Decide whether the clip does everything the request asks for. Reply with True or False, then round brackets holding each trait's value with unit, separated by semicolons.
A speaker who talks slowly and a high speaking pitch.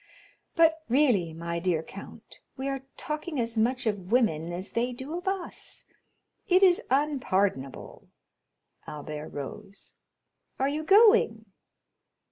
True (120 wpm; 240 Hz)